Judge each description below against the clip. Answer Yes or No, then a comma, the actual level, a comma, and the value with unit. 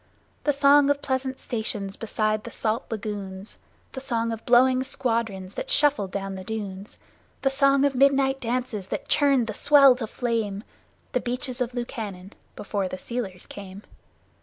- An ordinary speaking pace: Yes, average, 160 wpm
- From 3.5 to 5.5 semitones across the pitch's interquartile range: Yes, average, 4.7 semitones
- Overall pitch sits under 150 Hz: No, high, 235 Hz